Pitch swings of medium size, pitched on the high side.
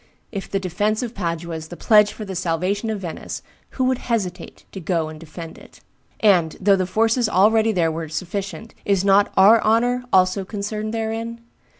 Yes: average, 3.9 semitones; high, 200 Hz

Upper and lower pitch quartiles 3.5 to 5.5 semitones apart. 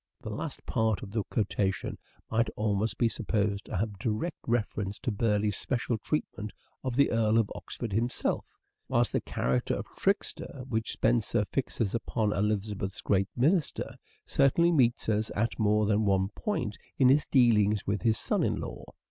No: narrow, 2.6 semitones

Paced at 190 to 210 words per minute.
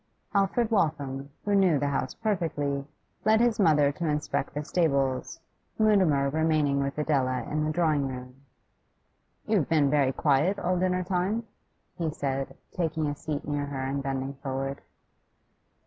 No: average, 145 wpm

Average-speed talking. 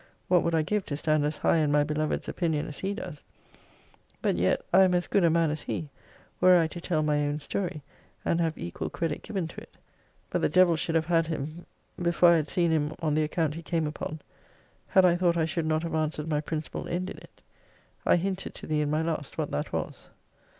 No: fast, 235 wpm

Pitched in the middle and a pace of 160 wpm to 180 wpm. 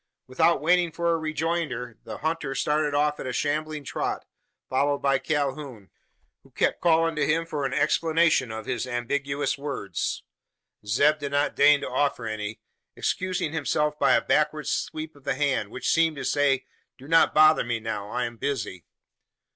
Yes: medium, 145 Hz; average, 170 wpm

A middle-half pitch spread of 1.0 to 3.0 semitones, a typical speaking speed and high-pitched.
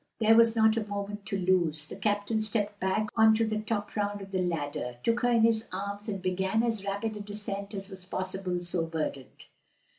No: narrow, 2.6 semitones; fast, 210 wpm; high, 205 Hz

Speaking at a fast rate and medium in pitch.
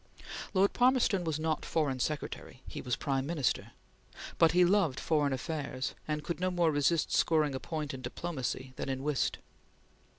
No: average, 165 wpm; medium, 155 Hz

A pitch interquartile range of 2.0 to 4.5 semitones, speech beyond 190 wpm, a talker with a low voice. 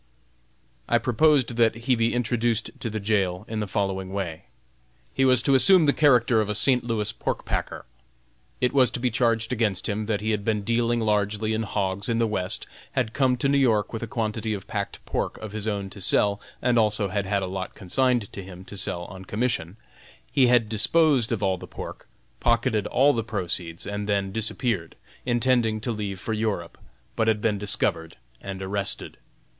Yes: average, 3.1 semitones; average, 200 wpm; low, 110 Hz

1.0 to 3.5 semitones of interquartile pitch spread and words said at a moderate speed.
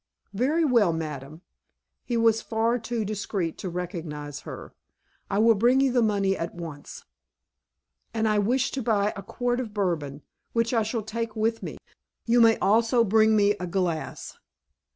No: average, 4.3 semitones; average, 165 wpm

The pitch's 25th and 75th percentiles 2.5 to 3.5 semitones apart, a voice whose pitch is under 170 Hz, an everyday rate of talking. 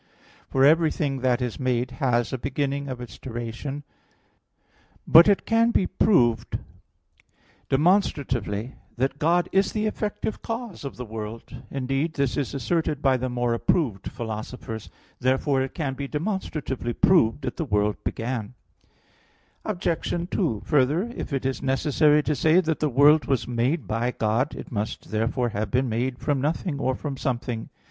No: average, 4.3 semitones; low, 135 Hz; average, 155 wpm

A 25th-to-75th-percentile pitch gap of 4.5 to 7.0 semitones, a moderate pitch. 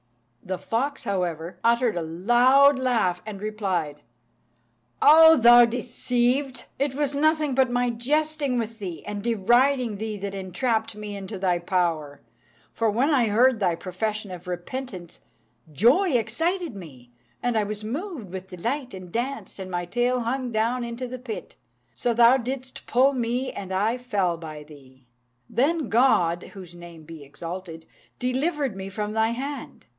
No: wide, 5.5 semitones; high, 225 Hz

